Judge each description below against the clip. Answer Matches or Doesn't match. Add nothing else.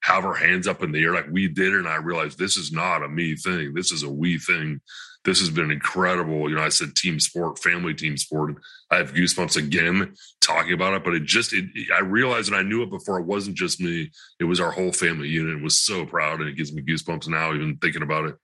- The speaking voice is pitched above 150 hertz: Doesn't match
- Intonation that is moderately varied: Matches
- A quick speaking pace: Matches